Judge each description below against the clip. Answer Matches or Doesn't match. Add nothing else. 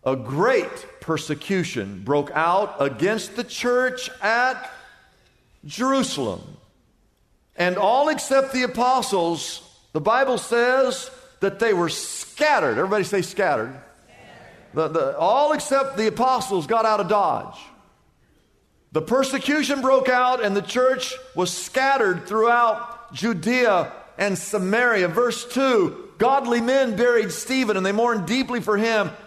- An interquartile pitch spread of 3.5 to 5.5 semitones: Matches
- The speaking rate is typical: Doesn't match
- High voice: Matches